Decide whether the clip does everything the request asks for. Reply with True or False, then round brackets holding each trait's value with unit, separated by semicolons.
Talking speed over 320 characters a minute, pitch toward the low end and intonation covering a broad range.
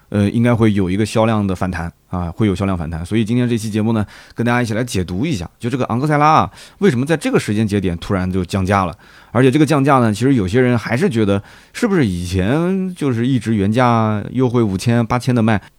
False (370 characters per minute; 110 Hz; 4.2 semitones)